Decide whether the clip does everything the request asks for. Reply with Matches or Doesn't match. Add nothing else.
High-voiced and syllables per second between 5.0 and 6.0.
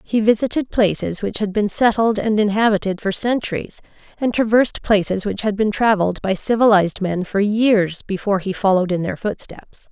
Matches